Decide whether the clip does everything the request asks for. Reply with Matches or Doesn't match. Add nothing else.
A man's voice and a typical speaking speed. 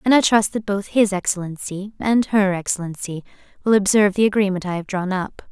Doesn't match